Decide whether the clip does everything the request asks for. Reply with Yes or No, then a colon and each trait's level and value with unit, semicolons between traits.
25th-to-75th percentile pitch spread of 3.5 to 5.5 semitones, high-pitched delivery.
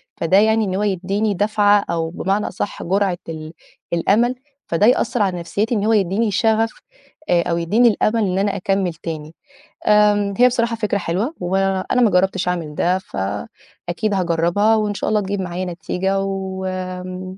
No: average, 2.8 semitones; high, 195 Hz